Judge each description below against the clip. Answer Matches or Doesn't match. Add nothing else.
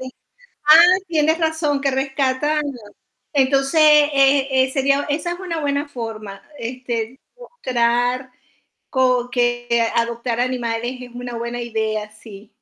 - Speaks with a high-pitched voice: Matches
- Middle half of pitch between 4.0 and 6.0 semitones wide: Doesn't match